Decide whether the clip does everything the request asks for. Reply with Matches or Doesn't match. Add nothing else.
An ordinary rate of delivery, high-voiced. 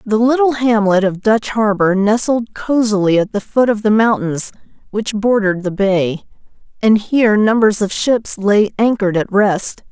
Matches